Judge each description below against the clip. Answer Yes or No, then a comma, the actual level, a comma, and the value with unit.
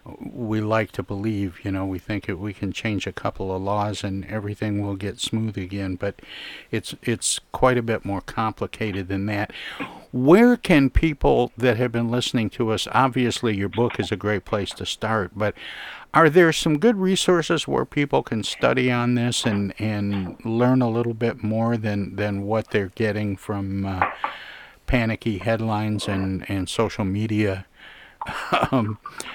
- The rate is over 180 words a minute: No, average, 170 wpm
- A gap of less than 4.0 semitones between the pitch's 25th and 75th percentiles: Yes, average, 3.2 semitones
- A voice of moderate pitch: No, low, 110 Hz